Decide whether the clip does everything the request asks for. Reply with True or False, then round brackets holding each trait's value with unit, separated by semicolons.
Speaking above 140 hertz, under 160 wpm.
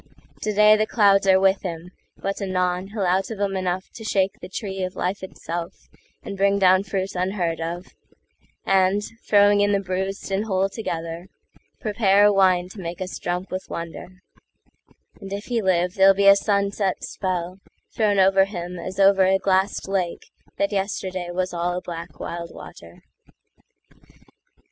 True (190 Hz; 150 wpm)